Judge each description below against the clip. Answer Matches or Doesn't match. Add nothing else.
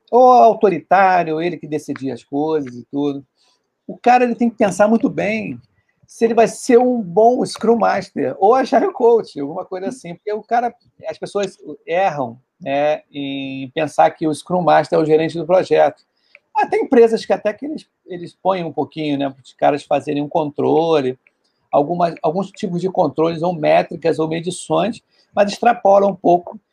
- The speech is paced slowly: Doesn't match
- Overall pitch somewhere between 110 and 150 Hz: Doesn't match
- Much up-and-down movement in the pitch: Matches